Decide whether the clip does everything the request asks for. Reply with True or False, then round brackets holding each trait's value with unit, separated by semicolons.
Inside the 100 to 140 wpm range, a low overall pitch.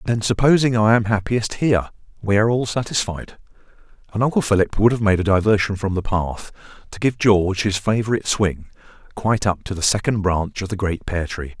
False (195 wpm; 105 Hz)